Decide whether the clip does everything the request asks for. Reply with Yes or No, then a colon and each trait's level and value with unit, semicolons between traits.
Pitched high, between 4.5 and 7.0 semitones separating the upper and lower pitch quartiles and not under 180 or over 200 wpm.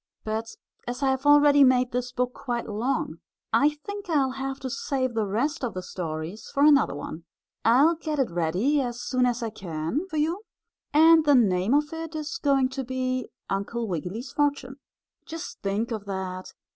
Yes: very high, 255 Hz; average, 5.0 semitones; average, 185 wpm